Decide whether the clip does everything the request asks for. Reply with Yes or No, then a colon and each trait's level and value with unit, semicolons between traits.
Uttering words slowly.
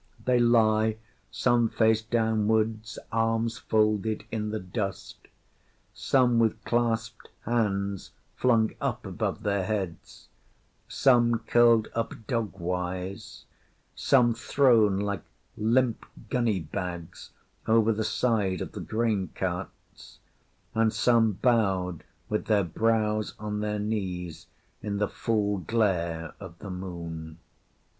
Yes: slow, 115 wpm